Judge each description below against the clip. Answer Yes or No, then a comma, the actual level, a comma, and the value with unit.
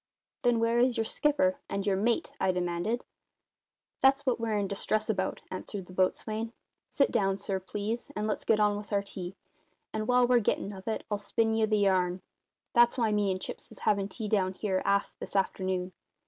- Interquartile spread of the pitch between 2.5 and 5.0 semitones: Yes, average, 3.1 semitones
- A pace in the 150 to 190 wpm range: No, average, 200 wpm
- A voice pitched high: Yes, high, 210 Hz